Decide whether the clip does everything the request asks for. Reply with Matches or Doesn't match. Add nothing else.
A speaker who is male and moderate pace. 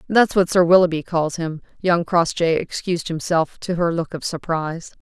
Doesn't match